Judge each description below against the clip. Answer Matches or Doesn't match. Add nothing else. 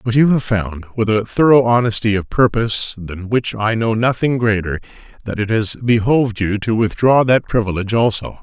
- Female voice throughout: Doesn't match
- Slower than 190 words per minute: Matches